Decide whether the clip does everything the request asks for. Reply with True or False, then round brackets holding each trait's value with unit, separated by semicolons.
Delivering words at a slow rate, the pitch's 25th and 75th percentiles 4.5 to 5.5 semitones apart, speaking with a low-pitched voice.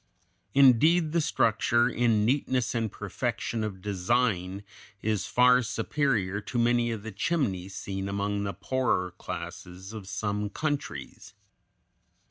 False (120 wpm; 4.0 semitones; 110 Hz)